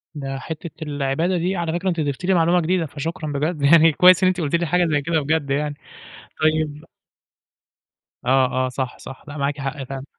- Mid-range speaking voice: Yes, medium, 155 Hz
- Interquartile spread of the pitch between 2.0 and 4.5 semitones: Yes, average, 3.3 semitones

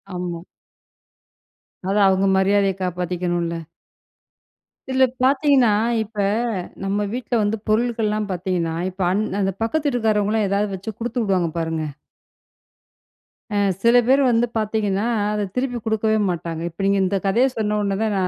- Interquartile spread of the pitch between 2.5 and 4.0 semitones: Yes, average, 3.3 semitones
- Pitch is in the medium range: No, high, 205 Hz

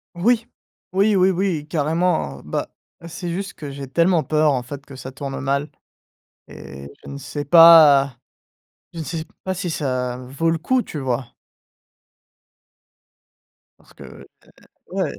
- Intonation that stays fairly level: No, average, 4.3 semitones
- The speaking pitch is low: No, medium, 155 Hz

